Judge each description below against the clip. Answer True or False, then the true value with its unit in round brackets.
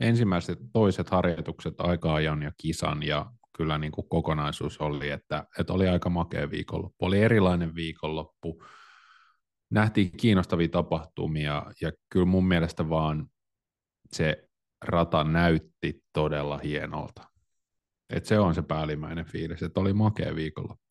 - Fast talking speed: False (125 wpm)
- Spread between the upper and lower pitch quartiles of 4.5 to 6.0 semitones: False (2.8 semitones)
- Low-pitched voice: True (85 Hz)